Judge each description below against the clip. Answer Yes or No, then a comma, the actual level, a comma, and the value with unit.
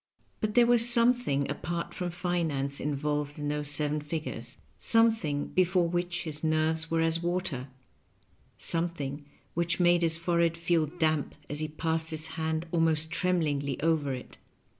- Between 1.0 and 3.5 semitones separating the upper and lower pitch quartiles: Yes, average, 2.7 semitones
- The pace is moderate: Yes, average, 150 wpm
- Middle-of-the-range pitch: Yes, medium, 160 Hz